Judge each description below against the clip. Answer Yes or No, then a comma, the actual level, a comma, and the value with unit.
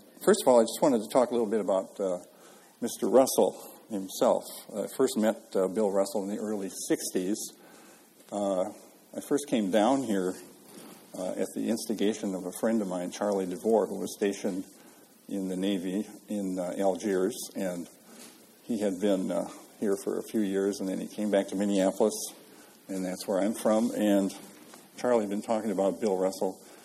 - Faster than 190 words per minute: No, average, 185 wpm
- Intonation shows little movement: Yes, narrow, 1.8 semitones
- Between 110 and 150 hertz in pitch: No, low, 100 Hz